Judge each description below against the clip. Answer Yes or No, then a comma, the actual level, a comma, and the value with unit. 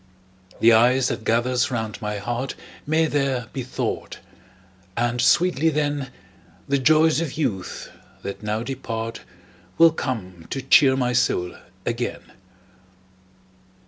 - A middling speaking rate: No, slow, 120 wpm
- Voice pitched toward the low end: Yes, low, 125 Hz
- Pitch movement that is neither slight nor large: Yes, average, 3.8 semitones